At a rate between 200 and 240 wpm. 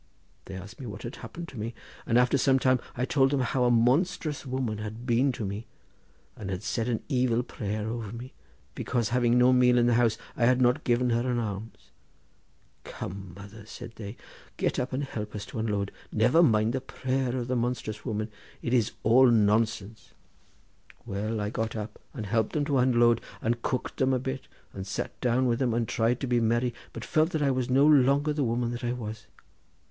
Yes: fast, 205 wpm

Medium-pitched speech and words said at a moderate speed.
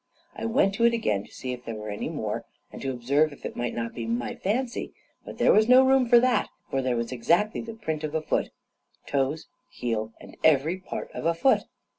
No: medium, 155 Hz; fast, 230 wpm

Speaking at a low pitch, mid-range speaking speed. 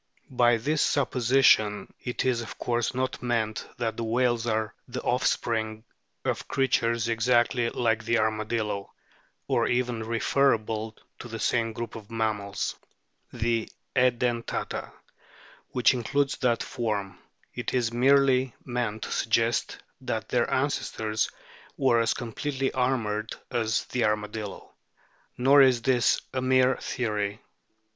No: low, 115 Hz; slow, 125 wpm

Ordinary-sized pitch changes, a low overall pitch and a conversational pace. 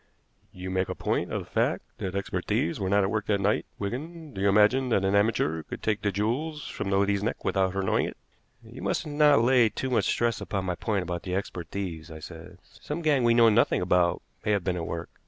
No: average, 4.1 semitones; low, 100 Hz; fast, 245 wpm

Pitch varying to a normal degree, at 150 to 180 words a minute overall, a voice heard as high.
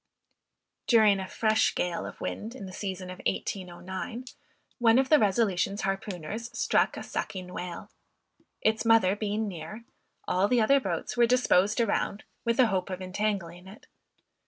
Yes: average, 3.6 semitones; average, 155 wpm; high, 200 Hz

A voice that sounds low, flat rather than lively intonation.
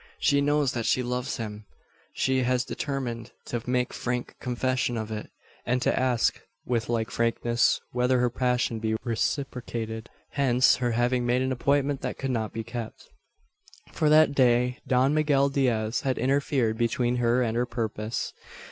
Yes: low, 125 Hz; narrow, 2.0 semitones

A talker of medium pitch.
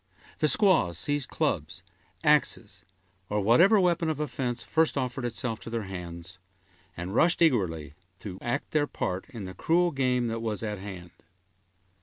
No: low, 120 Hz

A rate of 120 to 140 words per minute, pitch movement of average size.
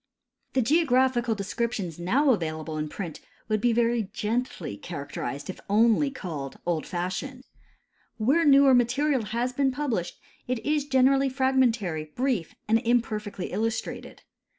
No: slow, 135 wpm; wide, 6.0 semitones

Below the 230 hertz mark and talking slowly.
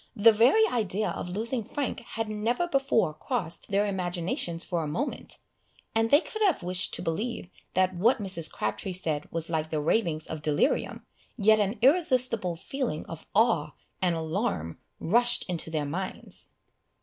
No: high, 190 Hz; average, 160 wpm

